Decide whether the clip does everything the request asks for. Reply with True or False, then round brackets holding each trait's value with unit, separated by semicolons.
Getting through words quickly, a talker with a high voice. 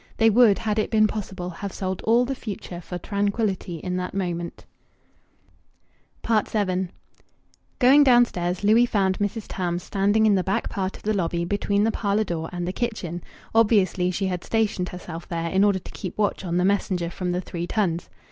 False (185 wpm; 195 Hz)